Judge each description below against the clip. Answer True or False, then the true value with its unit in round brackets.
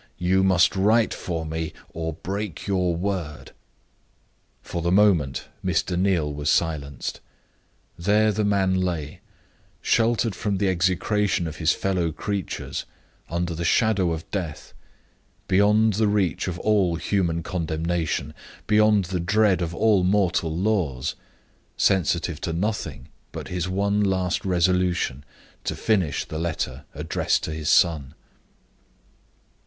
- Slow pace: True (125 wpm)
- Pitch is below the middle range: True (90 Hz)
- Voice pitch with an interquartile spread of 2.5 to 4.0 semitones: True (3.6 semitones)